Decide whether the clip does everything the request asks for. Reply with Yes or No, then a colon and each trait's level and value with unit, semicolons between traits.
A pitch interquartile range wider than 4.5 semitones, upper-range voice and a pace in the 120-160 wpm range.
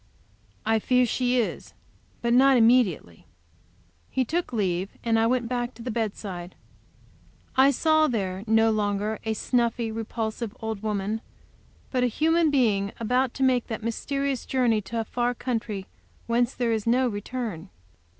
No: average, 2.7 semitones; high, 230 Hz; average, 150 wpm